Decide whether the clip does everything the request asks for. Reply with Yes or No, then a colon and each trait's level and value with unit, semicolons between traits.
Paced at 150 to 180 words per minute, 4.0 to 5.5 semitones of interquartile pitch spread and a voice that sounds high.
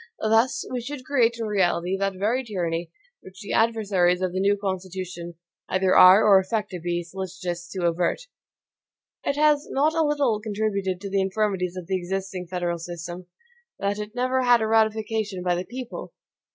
No: average, 175 wpm; average, 3.6 semitones; high, 195 Hz